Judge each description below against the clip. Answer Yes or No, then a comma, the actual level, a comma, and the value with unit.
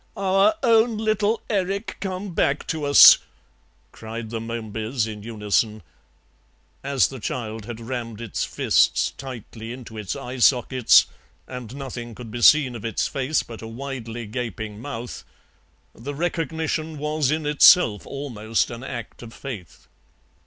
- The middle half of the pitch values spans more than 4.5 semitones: Yes, average, 4.9 semitones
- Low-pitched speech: Yes, low, 125 Hz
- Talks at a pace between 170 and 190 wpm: No, average, 140 wpm